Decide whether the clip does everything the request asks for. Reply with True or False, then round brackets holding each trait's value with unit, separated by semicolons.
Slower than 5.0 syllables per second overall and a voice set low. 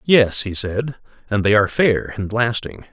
True (4.5 syllables/s; 110 Hz)